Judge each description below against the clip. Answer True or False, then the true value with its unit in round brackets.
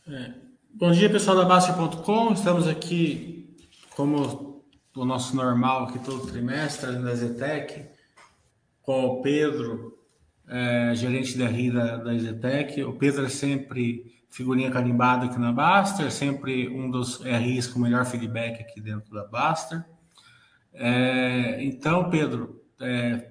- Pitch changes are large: False (3.4 semitones)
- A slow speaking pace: False (135 wpm)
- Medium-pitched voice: False (130 Hz)